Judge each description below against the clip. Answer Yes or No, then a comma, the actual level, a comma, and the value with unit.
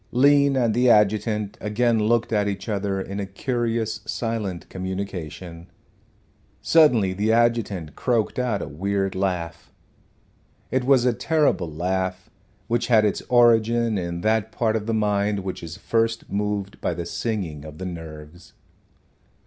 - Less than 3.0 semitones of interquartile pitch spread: No, average, 3.8 semitones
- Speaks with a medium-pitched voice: No, low, 105 Hz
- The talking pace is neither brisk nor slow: Yes, average, 145 wpm